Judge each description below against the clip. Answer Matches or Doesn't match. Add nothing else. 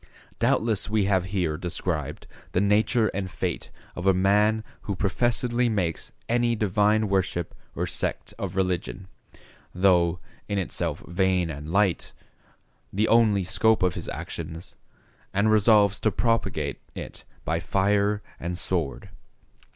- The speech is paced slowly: Matches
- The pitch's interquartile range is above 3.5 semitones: Doesn't match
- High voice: Doesn't match